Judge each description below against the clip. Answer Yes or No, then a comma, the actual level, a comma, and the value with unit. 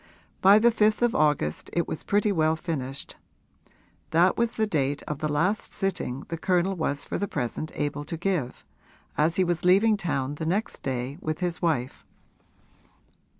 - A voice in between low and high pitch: Yes, medium, 165 Hz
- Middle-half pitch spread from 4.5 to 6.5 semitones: Yes, average, 4.9 semitones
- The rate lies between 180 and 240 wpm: No, average, 170 wpm